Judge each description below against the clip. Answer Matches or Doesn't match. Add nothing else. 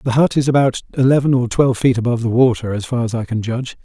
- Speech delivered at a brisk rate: Matches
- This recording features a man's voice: Matches